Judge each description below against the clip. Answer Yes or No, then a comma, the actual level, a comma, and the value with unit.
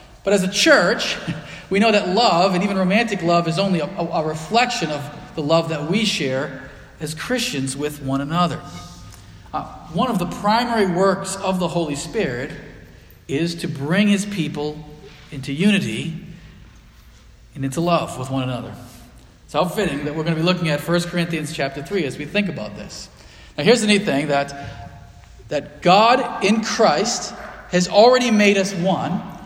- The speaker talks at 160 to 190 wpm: Yes, average, 175 wpm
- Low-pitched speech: No, medium, 170 Hz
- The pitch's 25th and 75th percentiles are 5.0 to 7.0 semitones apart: Yes, average, 5.3 semitones